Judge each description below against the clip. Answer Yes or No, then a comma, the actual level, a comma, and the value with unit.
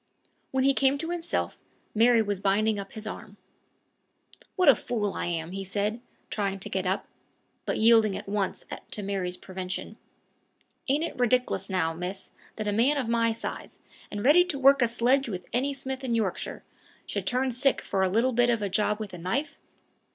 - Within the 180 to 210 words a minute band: Yes, average, 190 wpm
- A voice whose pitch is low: No, high, 220 Hz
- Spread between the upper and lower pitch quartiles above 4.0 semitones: Yes, average, 4.9 semitones